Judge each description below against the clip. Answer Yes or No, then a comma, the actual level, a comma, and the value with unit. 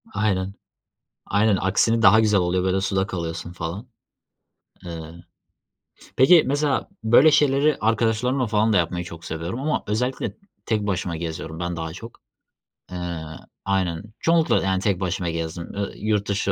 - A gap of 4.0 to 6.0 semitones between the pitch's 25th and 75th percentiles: Yes, average, 4.4 semitones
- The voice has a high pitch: No, very low, 95 Hz